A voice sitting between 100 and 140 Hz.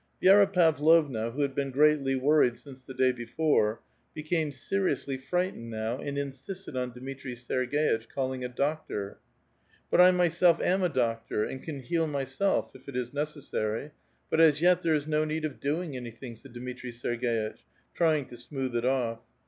Yes: low, 135 Hz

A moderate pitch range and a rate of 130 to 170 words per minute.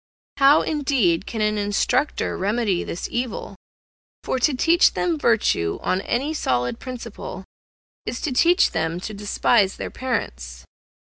No: wide, 6.4 semitones; slow, 135 wpm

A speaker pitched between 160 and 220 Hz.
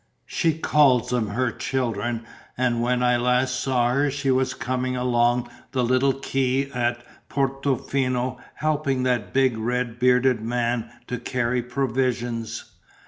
No: low, 125 Hz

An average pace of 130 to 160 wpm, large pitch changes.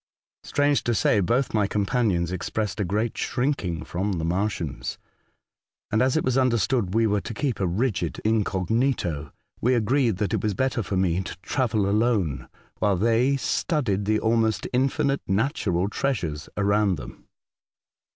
No: average, 155 wpm; average, 4.8 semitones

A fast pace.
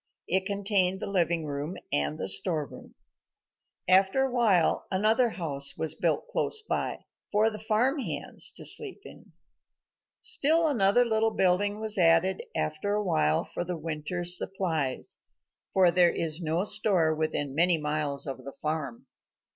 No: average, 145 wpm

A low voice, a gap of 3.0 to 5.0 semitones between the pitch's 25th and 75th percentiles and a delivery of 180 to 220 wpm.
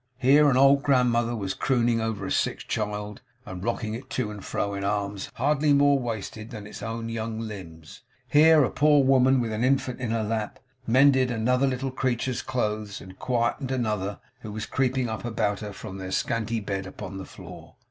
Yes: low, 115 Hz; average, 3.8 semitones; average, 190 wpm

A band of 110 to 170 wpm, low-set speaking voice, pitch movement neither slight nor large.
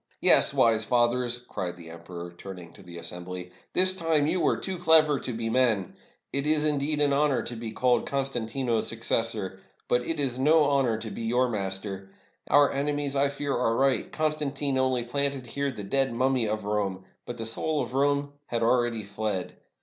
No: average, 195 wpm; low, 125 Hz; average, 4.5 semitones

